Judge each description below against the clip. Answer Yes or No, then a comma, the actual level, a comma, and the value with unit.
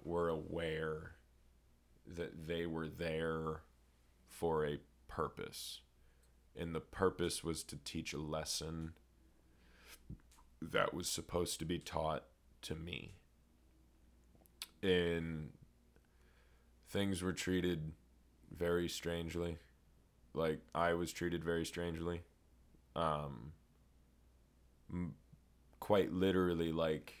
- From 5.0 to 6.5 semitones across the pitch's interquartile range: Yes, average, 5.3 semitones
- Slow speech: Yes, slow, 95 wpm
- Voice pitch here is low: Yes, very low, 80 Hz